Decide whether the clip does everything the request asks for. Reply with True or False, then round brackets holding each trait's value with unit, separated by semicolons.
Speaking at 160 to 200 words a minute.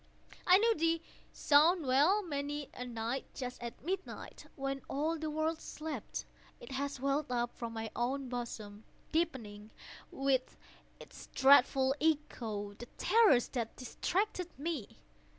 False (135 wpm)